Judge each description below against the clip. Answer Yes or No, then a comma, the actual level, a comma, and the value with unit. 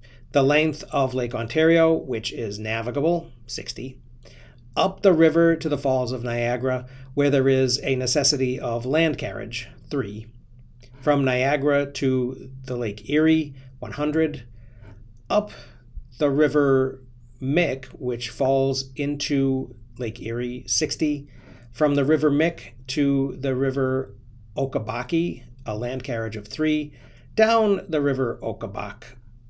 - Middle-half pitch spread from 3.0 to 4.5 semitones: Yes, average, 3.4 semitones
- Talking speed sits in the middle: No, slow, 120 wpm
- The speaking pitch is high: No, low, 130 Hz